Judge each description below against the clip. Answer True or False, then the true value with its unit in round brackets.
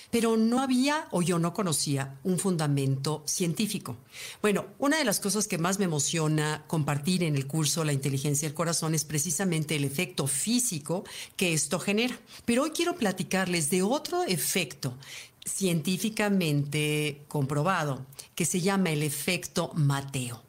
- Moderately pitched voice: True (170 Hz)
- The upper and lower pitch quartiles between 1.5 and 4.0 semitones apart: False (4.9 semitones)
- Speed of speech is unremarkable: True (145 wpm)